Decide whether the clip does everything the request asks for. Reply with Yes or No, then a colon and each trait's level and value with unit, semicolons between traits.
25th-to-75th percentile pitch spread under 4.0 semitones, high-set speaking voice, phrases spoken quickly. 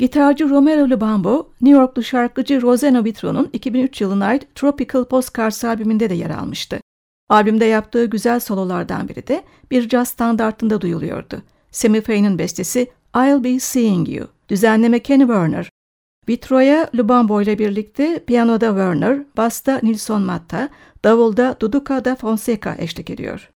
No: average, 3.2 semitones; high, 235 Hz; average, 130 wpm